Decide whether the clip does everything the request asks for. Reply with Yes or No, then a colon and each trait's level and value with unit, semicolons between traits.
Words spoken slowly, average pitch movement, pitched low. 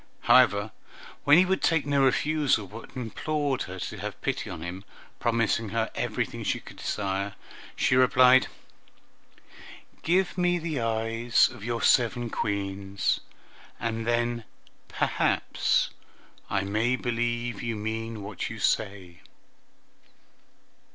Yes: slow, 120 wpm; average, 3.8 semitones; low, 115 Hz